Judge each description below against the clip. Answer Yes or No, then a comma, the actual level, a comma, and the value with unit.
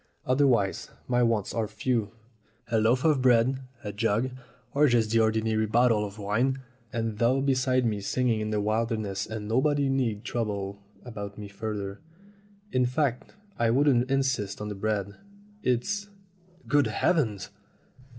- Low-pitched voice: Yes, low, 115 Hz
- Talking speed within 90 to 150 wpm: Yes, average, 145 wpm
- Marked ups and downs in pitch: No, average, 3.5 semitones